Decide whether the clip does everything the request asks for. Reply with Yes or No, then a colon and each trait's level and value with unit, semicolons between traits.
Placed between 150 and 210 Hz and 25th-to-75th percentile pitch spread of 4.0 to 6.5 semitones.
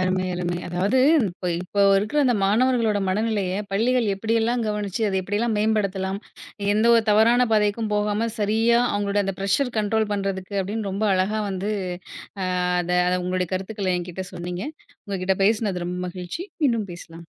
No: high, 205 Hz; average, 2.9 semitones